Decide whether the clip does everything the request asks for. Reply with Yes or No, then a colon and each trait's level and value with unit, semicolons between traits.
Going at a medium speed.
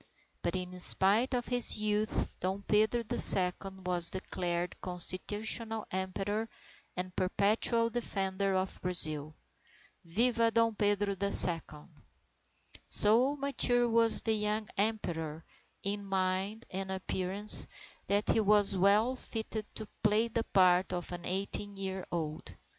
No: slow, 125 wpm